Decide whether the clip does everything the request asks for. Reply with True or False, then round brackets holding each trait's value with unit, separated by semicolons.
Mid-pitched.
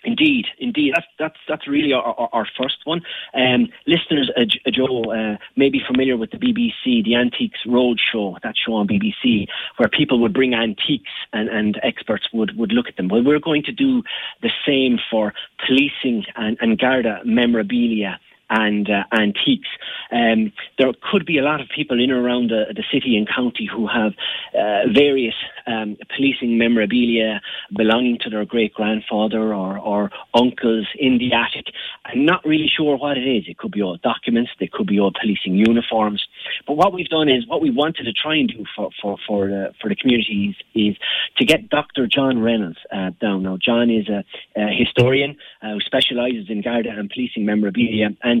False (120 Hz)